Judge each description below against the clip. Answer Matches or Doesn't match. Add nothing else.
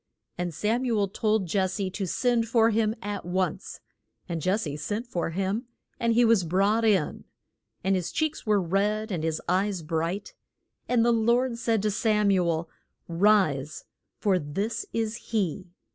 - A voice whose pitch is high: Matches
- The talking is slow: Doesn't match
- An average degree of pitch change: Matches